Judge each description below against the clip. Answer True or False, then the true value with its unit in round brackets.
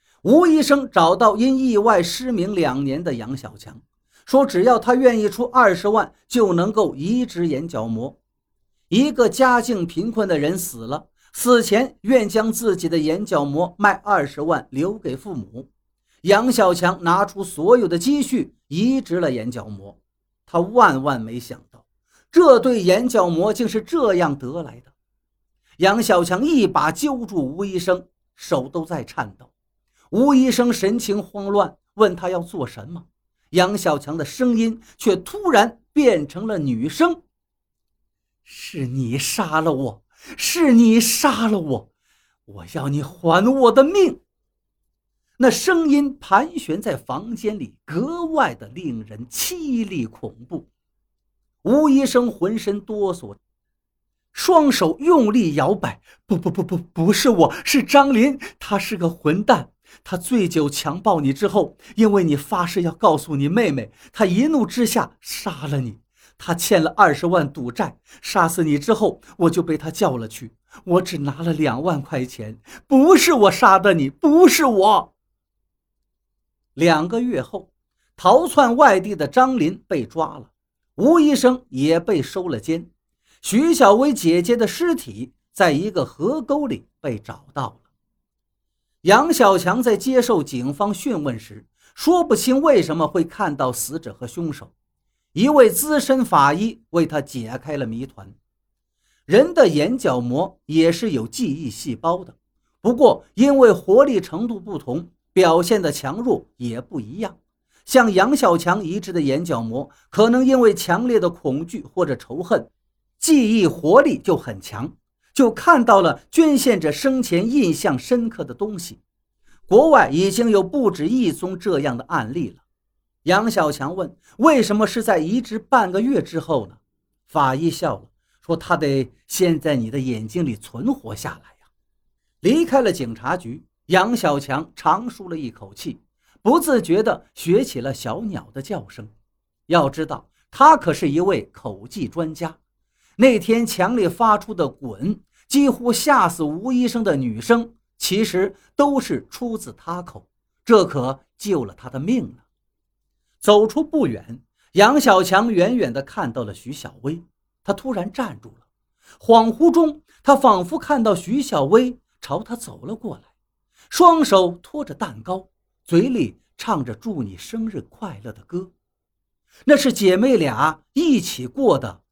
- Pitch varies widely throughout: True (8.6 semitones)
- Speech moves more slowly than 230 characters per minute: True (215 characters per minute)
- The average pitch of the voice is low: False (185 Hz)